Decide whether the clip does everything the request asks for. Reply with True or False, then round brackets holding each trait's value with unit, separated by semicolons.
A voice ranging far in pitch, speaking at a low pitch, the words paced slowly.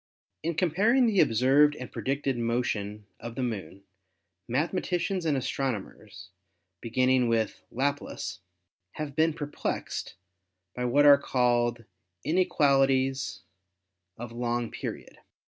False (3.9 semitones; 130 Hz; 110 wpm)